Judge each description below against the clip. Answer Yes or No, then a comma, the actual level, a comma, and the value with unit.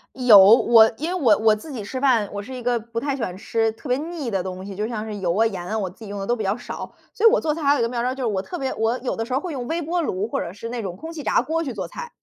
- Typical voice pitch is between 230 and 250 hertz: Yes, high, 235 Hz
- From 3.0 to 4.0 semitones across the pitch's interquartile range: No, average, 5.0 semitones